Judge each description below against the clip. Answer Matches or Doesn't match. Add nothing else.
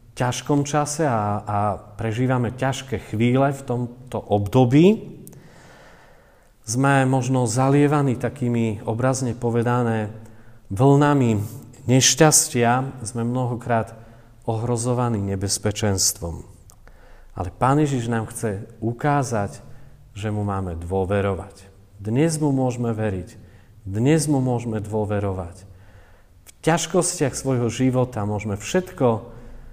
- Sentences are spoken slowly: Matches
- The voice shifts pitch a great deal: Doesn't match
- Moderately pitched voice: Doesn't match